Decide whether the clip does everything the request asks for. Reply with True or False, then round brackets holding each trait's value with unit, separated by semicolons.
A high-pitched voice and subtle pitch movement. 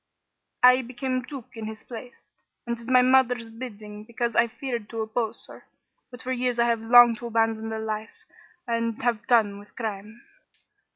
True (230 Hz; 2.0 semitones)